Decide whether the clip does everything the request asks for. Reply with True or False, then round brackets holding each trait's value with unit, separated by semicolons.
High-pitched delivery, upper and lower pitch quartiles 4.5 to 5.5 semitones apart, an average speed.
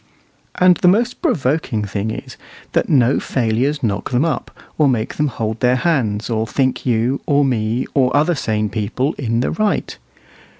False (130 Hz; 5.0 semitones; 170 wpm)